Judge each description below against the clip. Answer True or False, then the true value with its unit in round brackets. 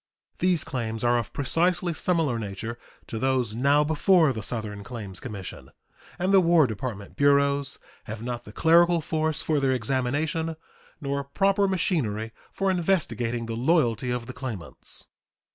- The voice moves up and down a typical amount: False (5.9 semitones)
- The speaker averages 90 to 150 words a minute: True (145 wpm)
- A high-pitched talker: False (135 Hz)